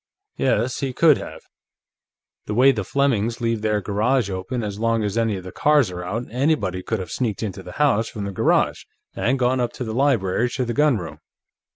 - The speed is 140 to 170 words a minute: No, fast, 205 wpm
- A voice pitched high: No, low, 115 Hz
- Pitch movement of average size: Yes, average, 4.1 semitones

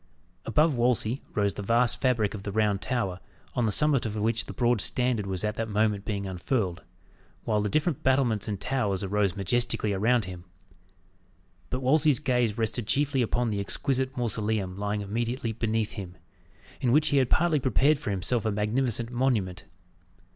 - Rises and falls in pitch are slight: No, average, 3.6 semitones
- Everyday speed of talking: Yes, average, 170 wpm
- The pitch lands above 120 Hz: No, low, 115 Hz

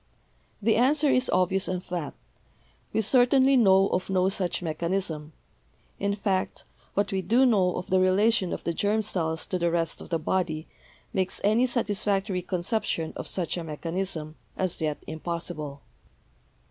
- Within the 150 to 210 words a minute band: Yes, average, 155 wpm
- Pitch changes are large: No, average, 3.4 semitones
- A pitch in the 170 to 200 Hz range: Yes, medium, 185 Hz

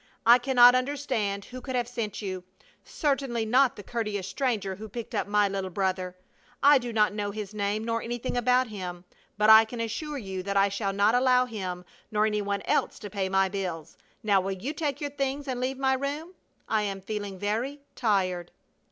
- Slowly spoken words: No, average, 200 wpm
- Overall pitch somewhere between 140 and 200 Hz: No, high, 215 Hz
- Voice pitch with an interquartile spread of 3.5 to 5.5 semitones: Yes, average, 4.2 semitones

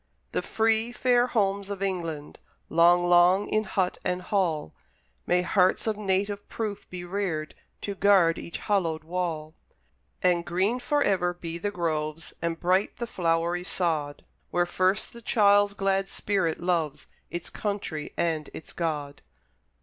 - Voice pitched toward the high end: No, medium, 180 Hz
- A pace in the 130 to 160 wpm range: Yes, average, 145 wpm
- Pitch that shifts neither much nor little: Yes, average, 3.3 semitones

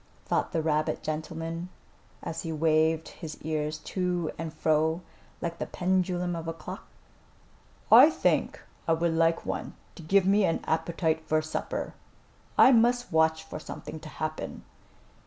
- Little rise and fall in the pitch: Yes, narrow, 2.1 semitones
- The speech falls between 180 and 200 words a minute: No, average, 150 wpm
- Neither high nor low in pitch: Yes, medium, 165 Hz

